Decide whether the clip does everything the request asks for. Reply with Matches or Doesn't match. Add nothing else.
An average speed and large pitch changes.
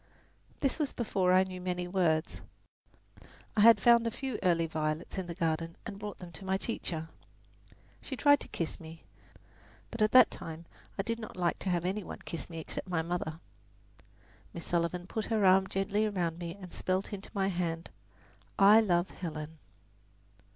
Doesn't match